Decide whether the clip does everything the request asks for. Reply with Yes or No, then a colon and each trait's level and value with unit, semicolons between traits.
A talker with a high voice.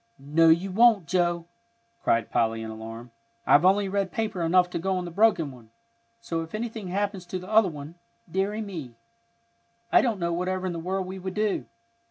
No: medium, 180 Hz